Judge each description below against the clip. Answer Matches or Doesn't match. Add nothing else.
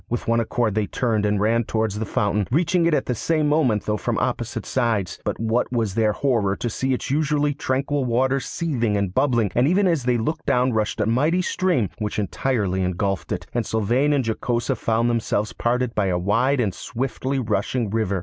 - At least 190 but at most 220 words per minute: Matches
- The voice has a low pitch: Matches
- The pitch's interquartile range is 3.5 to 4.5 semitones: Matches